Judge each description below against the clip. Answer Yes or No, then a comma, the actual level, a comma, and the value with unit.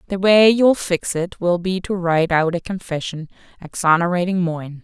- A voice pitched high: No, medium, 180 Hz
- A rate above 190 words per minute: No, average, 175 wpm